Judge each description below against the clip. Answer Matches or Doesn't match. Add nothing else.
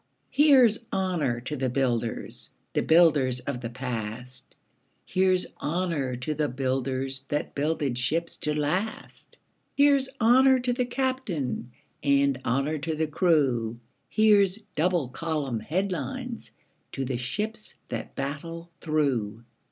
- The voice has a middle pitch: Matches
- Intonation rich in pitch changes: Matches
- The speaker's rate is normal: Doesn't match